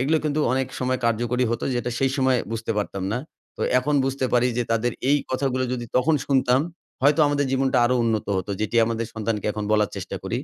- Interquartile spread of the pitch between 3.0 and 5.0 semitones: No, narrow, 2.6 semitones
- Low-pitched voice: Yes, low, 125 Hz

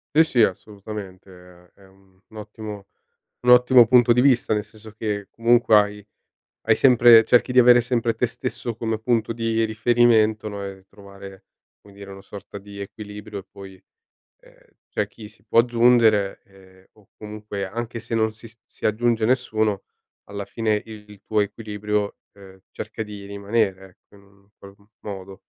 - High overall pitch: No, low, 105 Hz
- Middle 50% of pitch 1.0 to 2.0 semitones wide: No, narrow, 2.5 semitones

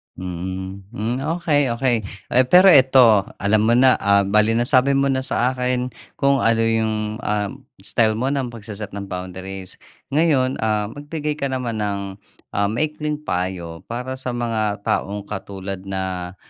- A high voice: No, low, 115 Hz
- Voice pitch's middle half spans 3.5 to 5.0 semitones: Yes, average, 4.6 semitones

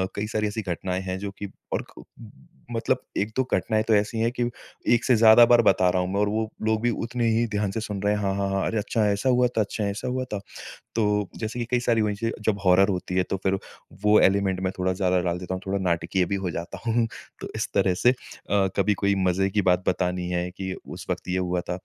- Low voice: Yes, low, 100 Hz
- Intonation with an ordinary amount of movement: Yes, average, 3.1 semitones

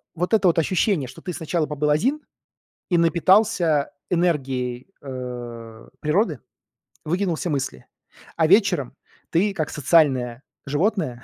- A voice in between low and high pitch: Yes, medium, 155 Hz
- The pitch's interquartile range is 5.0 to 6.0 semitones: Yes, average, 5.3 semitones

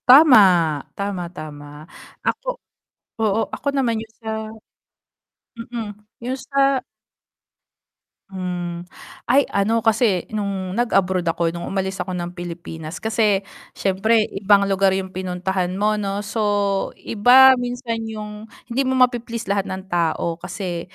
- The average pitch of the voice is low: No, high, 200 Hz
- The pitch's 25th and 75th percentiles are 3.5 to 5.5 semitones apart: Yes, average, 3.8 semitones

